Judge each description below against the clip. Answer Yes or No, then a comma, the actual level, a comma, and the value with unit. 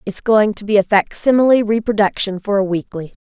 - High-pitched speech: Yes, high, 205 Hz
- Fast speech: No, average, 185 wpm